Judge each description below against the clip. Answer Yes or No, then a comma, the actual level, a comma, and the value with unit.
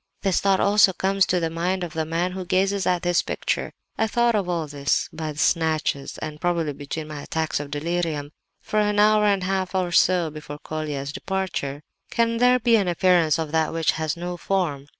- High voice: No, medium, 175 Hz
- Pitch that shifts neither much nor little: Yes, average, 3.6 semitones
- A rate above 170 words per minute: Yes, average, 195 wpm